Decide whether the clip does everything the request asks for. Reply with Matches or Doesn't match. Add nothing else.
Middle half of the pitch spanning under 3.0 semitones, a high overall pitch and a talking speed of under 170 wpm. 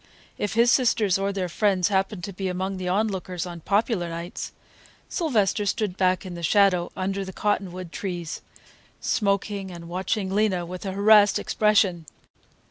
Matches